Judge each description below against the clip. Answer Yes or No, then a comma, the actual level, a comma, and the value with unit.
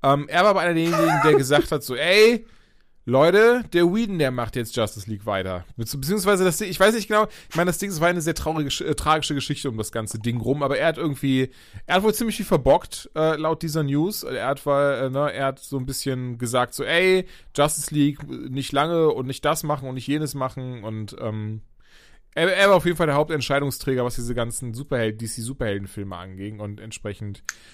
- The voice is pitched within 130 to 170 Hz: Yes, medium, 140 Hz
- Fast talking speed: Yes, fast, 220 wpm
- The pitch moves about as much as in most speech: No, wide, 5.7 semitones